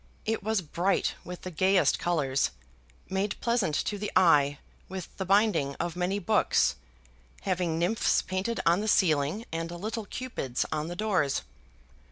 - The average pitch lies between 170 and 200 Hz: Yes, medium, 185 Hz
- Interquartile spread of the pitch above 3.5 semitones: Yes, average, 4.0 semitones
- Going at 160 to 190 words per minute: No, average, 150 wpm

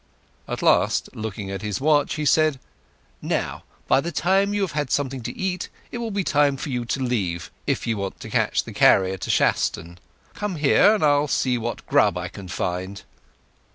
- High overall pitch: No, low, 135 Hz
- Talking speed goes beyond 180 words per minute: Yes, average, 195 wpm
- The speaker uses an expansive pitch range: Yes, wide, 7.9 semitones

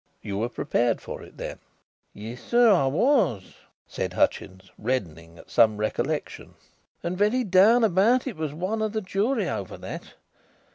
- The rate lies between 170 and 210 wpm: No, average, 155 wpm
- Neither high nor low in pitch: Yes, medium, 175 Hz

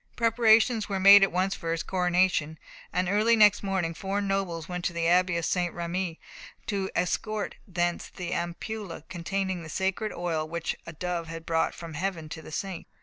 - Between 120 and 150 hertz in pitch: No, medium, 180 Hz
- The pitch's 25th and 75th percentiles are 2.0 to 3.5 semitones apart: Yes, narrow, 2.6 semitones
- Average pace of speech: Yes, average, 185 wpm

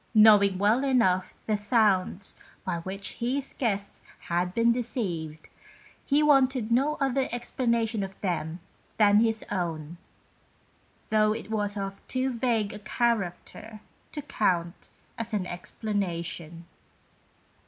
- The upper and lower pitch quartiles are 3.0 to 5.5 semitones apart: Yes, average, 4.1 semitones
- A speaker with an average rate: No, slow, 120 wpm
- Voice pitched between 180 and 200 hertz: No, high, 210 Hz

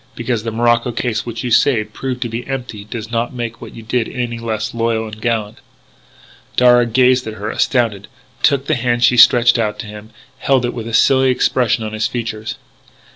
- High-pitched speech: No, low, 115 Hz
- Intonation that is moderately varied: No, narrow, 1.8 semitones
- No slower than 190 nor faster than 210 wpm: Yes, fast, 205 wpm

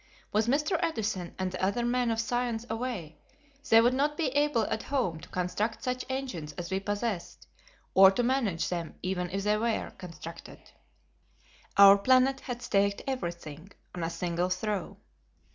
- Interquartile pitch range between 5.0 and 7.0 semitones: Yes, wide, 5.5 semitones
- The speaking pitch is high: Yes, high, 210 Hz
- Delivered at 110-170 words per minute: Yes, average, 160 wpm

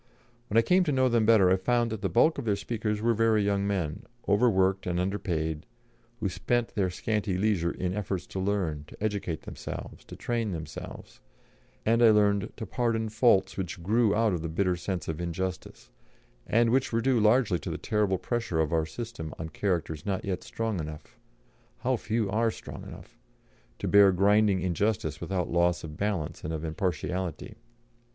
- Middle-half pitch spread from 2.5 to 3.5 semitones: No, average, 4.2 semitones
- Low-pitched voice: Yes, low, 100 Hz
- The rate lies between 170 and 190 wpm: Yes, average, 185 wpm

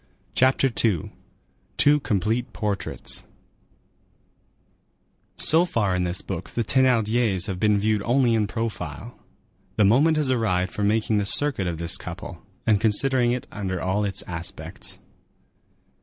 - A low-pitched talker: Yes, low, 110 Hz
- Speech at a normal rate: No, slow, 130 wpm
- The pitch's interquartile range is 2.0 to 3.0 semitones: No, average, 4.0 semitones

